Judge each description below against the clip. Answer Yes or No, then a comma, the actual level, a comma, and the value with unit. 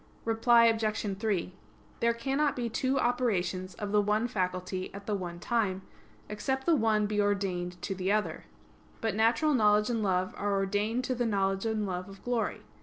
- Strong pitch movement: No, average, 3.2 semitones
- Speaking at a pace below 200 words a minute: Yes, average, 180 wpm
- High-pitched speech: Yes, high, 210 Hz